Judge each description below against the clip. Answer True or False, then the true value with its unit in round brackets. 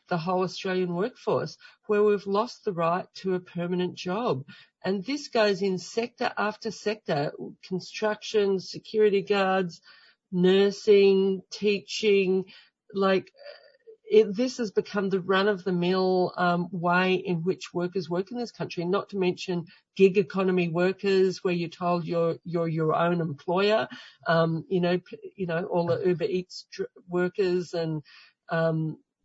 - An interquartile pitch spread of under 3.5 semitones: True (2.6 semitones)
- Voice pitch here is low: False (185 Hz)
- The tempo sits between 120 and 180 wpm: True (140 wpm)